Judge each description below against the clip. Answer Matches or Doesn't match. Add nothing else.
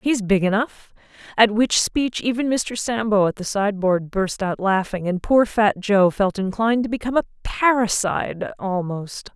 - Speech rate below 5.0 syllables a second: Matches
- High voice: Matches